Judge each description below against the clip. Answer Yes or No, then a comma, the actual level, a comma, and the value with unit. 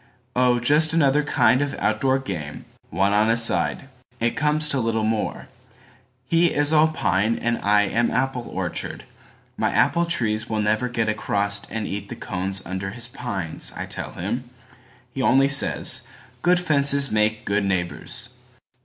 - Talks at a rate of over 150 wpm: No, average, 145 wpm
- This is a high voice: No, low, 120 Hz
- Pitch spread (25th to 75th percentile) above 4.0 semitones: Yes, average, 4.4 semitones